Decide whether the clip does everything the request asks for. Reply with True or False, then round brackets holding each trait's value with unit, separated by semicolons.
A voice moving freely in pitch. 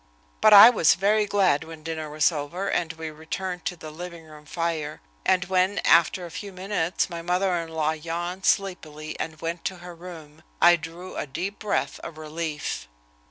False (2.7 semitones)